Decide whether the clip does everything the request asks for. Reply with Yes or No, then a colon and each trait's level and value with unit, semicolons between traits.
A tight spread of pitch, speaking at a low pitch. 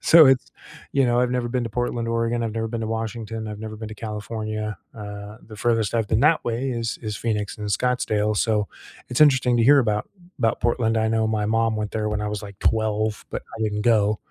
Yes: narrow, 1.8 semitones; low, 110 Hz